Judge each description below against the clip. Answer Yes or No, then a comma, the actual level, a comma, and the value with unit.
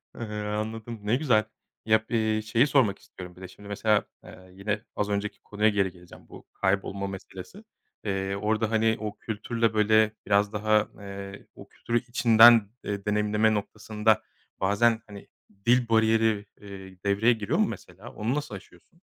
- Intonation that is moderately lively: No, narrow, 1.9 semitones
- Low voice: Yes, low, 105 Hz